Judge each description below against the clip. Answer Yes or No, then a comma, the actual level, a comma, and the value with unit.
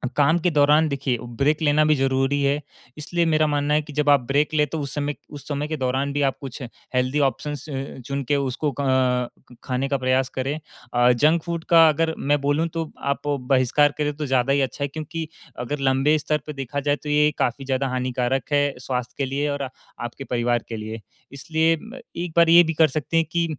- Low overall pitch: No, medium, 145 Hz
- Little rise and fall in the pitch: Yes, narrow, 2.3 semitones